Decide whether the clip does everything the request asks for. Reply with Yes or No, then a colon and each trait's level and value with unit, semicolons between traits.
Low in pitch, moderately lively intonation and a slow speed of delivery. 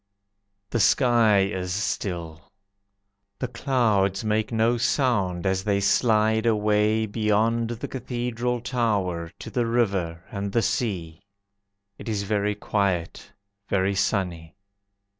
Yes: low, 105 Hz; average, 3.3 semitones; slow, 115 wpm